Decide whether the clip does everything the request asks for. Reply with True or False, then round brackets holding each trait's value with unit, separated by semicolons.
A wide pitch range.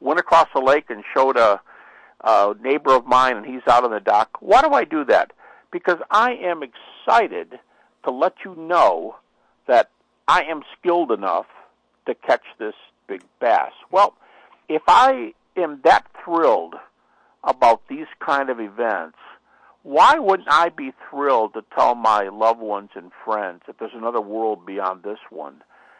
True (7.9 semitones)